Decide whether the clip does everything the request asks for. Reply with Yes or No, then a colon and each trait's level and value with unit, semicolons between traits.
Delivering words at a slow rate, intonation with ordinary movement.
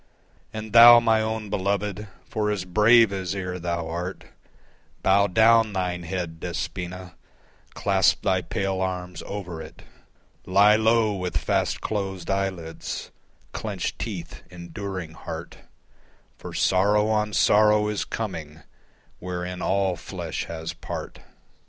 Yes: slow, 120 wpm; average, 3.0 semitones